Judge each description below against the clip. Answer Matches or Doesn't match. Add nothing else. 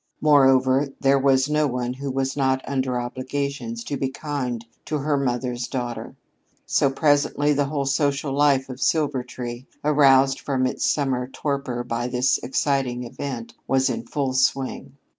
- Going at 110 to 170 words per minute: Matches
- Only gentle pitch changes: Matches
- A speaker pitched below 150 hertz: Matches